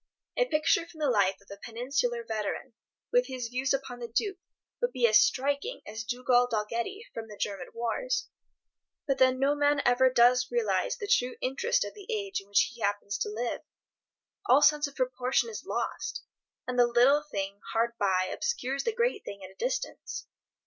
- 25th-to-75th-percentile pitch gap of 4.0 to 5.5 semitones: Yes, average, 4.9 semitones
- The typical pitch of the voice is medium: No, very high, 255 Hz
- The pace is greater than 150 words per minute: Yes, average, 185 wpm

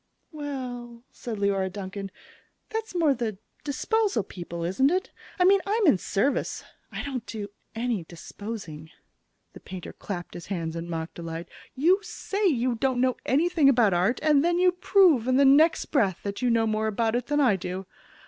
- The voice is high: Yes, high, 240 Hz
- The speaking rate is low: No, average, 175 wpm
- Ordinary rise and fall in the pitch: No, wide, 7.2 semitones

